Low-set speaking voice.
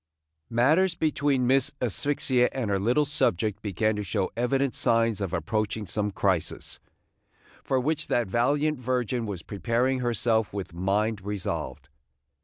Yes: low, 115 Hz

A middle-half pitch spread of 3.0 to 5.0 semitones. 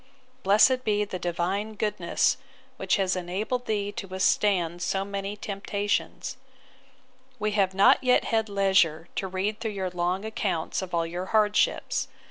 No: narrow, 2.4 semitones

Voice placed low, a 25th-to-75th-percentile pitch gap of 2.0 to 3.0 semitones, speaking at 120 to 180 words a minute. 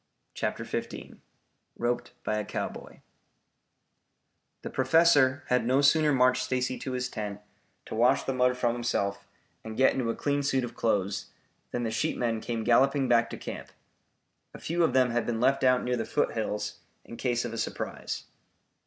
Yes: low, 125 Hz; narrow, 2.4 semitones; average, 170 wpm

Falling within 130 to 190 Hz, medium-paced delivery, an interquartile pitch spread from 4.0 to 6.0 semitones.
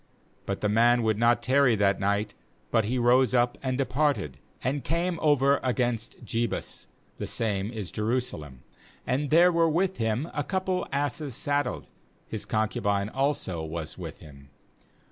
No: low, 120 Hz; average, 160 wpm; wide, 5.4 semitones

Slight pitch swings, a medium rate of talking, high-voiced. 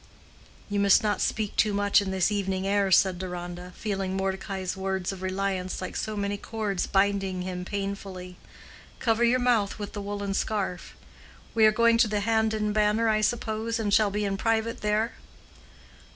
Yes: narrow, 2.2 semitones; average, 175 wpm; high, 200 Hz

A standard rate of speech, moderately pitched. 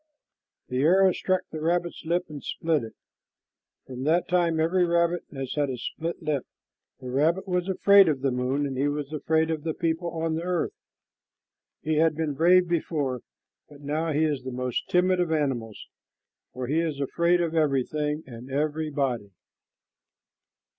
Yes: average, 165 wpm; medium, 155 Hz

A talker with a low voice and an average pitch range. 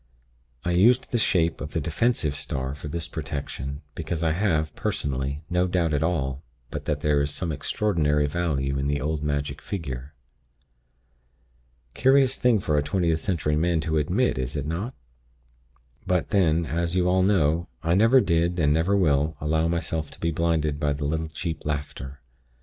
Yes: very low, 80 Hz; average, 3.1 semitones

